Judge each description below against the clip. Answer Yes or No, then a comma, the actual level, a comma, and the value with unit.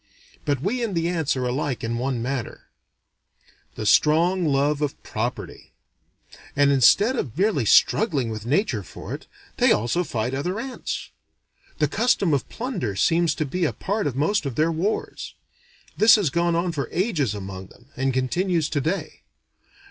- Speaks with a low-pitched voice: No, medium, 150 Hz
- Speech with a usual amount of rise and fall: No, wide, 5.9 semitones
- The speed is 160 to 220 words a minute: Yes, average, 165 wpm